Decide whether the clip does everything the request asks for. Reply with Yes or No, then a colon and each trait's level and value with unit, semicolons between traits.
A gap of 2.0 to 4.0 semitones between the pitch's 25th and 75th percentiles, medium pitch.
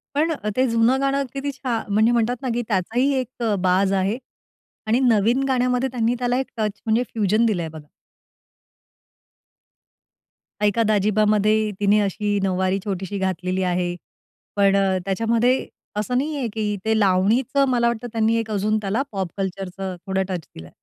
No: average, 3.7 semitones; high, 215 Hz